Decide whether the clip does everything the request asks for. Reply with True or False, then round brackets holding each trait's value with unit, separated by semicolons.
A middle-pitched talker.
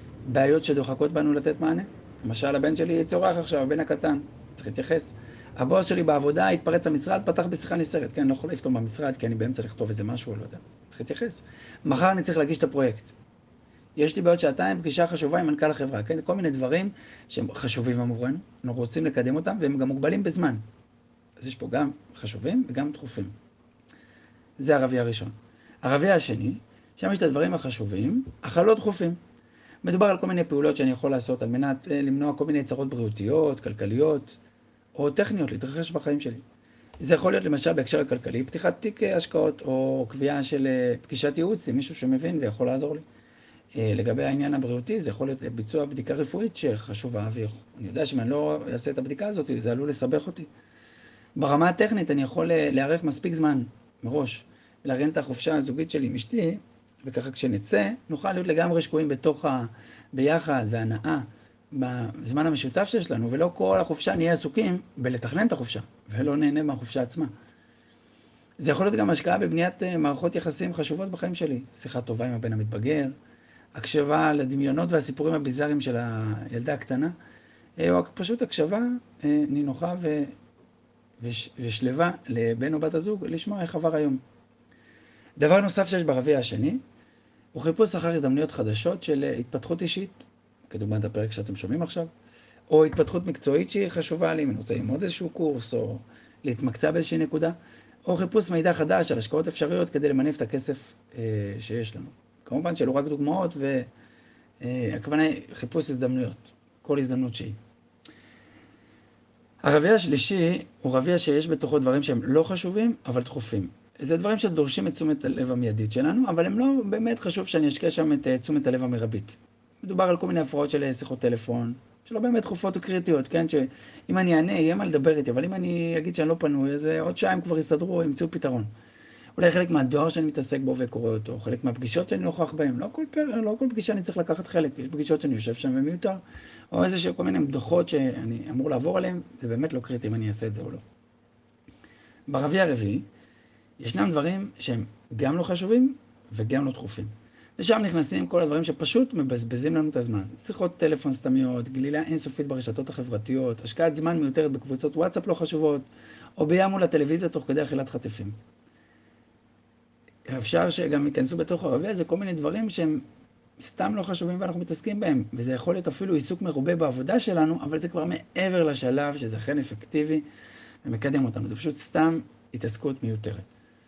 True (145 Hz)